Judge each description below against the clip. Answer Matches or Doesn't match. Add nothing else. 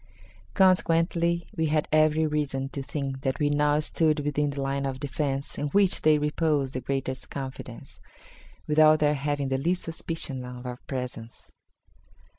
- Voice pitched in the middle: Matches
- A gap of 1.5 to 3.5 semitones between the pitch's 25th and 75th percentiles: Matches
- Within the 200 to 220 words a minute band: Doesn't match